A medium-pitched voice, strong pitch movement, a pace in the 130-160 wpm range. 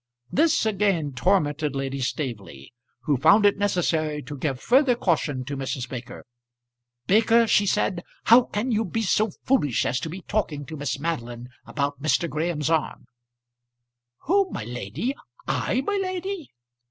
Yes: medium, 160 Hz; wide, 7.8 semitones; average, 150 wpm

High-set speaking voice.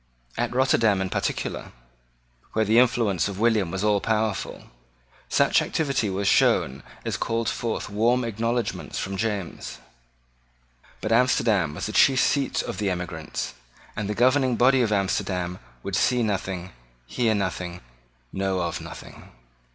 No: low, 105 Hz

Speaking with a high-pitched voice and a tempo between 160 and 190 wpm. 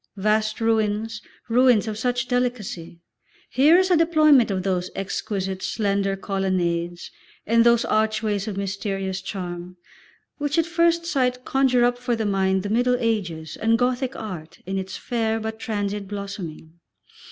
No: high, 215 Hz; average, 145 wpm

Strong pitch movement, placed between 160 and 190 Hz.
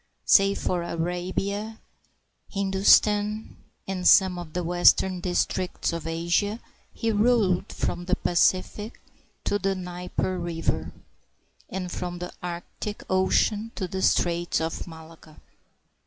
No: narrow, 2.4 semitones; medium, 185 Hz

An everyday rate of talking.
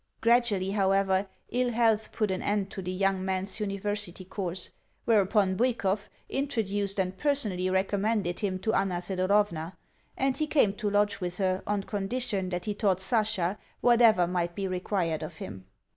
Yes: average, 160 wpm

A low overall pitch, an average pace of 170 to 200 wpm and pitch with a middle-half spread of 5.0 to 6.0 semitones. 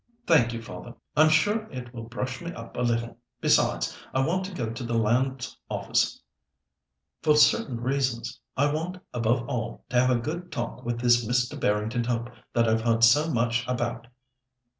No: low, 120 Hz; average, 180 wpm; average, 2.8 semitones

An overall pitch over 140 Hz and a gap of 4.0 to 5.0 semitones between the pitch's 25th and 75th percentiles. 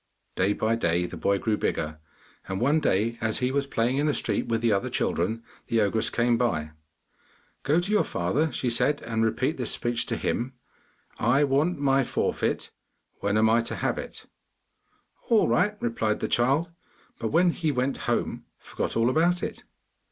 No: low, 120 Hz; average, 4.4 semitones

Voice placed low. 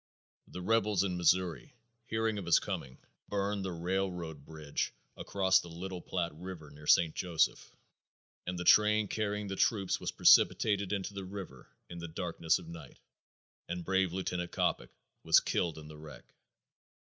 Yes: very low, 90 Hz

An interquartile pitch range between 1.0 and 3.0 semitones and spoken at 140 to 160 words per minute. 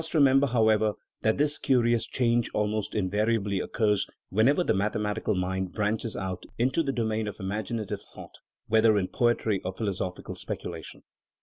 Yes: average, 2.7 semitones; average, 150 wpm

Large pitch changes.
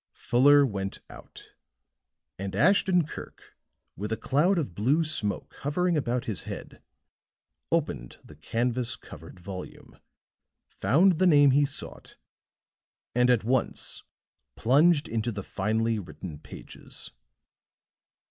Yes: wide, 6.5 semitones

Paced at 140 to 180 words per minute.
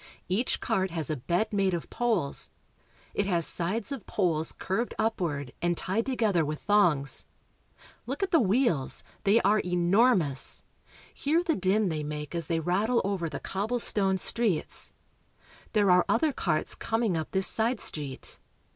Yes: average, 160 wpm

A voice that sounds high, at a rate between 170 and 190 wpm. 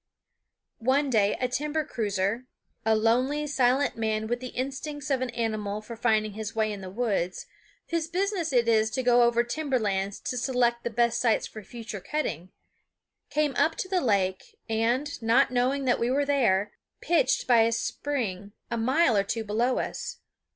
Yes: high, 235 Hz; average, 180 wpm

